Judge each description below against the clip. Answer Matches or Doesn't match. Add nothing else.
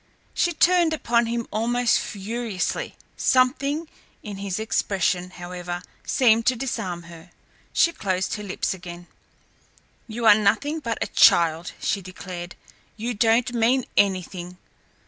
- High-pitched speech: Matches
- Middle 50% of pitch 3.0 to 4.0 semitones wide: Doesn't match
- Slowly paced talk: Matches